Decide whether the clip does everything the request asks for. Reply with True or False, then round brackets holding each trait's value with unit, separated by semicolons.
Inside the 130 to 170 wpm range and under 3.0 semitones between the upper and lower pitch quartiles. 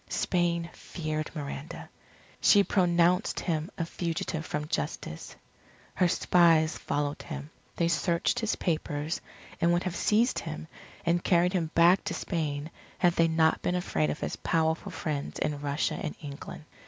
True (150 wpm; 2.5 semitones)